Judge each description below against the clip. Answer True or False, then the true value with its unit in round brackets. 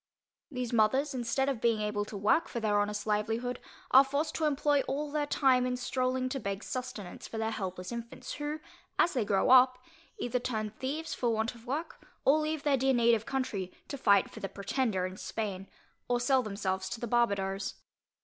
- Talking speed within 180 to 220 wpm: True (195 wpm)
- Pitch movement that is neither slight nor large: True (4.2 semitones)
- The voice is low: False (240 Hz)